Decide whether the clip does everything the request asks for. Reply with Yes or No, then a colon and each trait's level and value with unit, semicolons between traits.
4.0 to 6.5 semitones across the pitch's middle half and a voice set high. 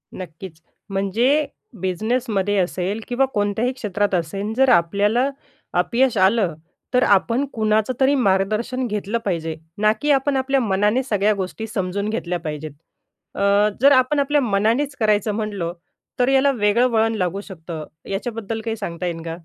Yes: average, 4.3 semitones; high, 210 Hz